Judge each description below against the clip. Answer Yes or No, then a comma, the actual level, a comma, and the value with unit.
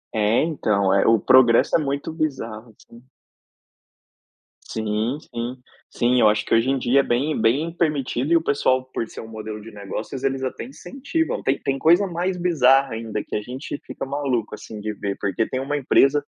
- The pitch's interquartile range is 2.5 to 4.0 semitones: No, average, 4.7 semitones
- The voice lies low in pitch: Yes, low, 130 Hz